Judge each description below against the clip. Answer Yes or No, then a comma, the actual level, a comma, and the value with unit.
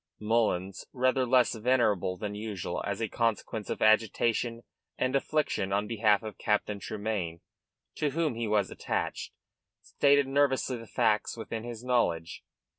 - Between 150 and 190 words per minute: No, average, 140 wpm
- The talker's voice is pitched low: Yes, low, 115 Hz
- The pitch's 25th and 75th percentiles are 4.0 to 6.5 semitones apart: No, average, 3.2 semitones